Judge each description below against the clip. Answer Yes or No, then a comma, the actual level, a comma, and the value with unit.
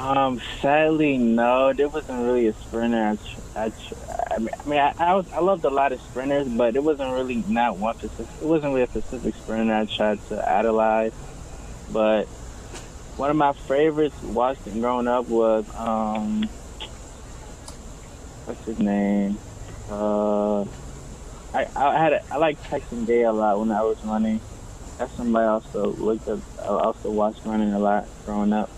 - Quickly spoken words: No, average, 170 wpm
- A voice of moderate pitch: No, low, 110 Hz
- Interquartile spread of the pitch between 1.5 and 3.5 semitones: Yes, average, 3.2 semitones